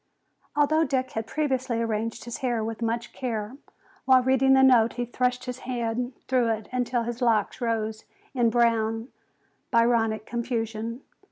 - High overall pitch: Yes, high, 235 Hz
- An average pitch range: No, narrow, 2.2 semitones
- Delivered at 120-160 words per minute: Yes, average, 150 wpm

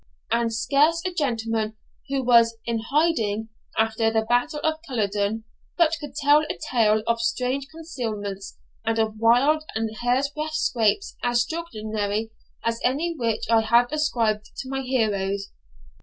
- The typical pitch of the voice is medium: No, high, 235 Hz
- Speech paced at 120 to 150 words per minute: Yes, average, 140 wpm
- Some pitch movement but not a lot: Yes, average, 4.3 semitones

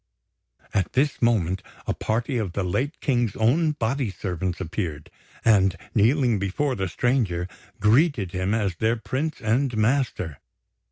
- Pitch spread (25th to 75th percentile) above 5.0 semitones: Yes, wide, 5.5 semitones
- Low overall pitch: Yes, low, 110 Hz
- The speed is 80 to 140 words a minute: Yes, slow, 135 wpm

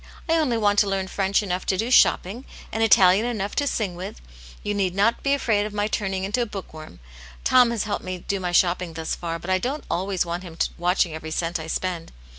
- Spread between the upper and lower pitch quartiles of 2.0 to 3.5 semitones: Yes, average, 3.1 semitones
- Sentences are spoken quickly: Yes, fast, 235 wpm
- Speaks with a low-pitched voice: No, high, 195 Hz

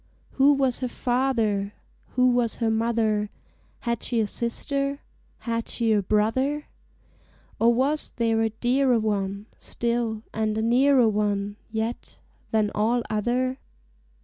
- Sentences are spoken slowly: Yes, slow, 130 wpm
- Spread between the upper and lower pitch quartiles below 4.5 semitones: Yes, average, 2.8 semitones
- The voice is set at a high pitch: Yes, high, 230 Hz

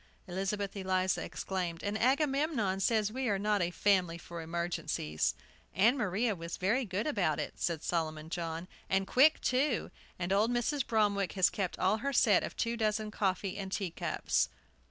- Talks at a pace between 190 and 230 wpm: No, average, 170 wpm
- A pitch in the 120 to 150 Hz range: No, high, 195 Hz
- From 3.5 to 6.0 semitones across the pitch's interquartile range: Yes, average, 3.9 semitones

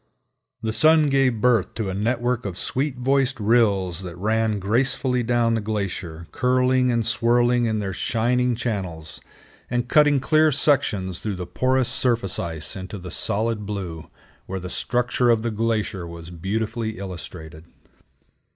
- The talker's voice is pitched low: Yes, low, 110 Hz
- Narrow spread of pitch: No, average, 4.5 semitones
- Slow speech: No, average, 150 wpm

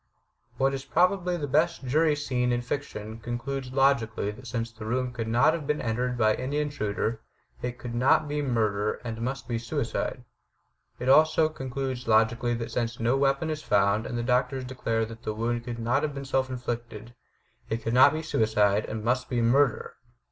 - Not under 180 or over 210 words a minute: Yes, average, 190 wpm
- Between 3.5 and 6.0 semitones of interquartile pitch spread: No, average, 3.0 semitones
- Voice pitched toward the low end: Yes, low, 125 Hz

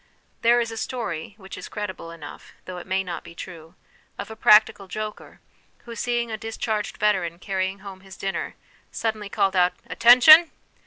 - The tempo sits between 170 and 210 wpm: Yes, average, 180 wpm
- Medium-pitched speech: No, high, 205 Hz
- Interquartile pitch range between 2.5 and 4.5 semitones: Yes, average, 3.3 semitones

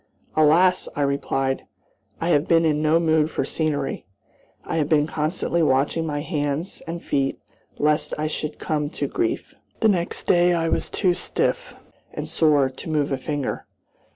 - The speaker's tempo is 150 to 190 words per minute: Yes, average, 165 wpm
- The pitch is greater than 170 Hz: No, medium, 155 Hz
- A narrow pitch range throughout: Yes, narrow, 2.3 semitones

